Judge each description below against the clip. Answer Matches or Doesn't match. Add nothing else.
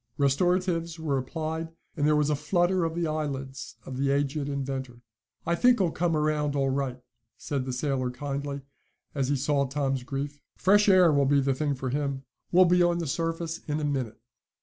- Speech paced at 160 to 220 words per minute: Matches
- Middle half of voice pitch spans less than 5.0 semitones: Matches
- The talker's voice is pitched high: Doesn't match